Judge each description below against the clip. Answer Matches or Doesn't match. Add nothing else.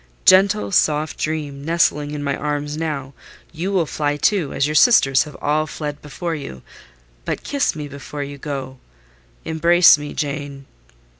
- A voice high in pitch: Doesn't match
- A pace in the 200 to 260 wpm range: Doesn't match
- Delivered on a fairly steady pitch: Matches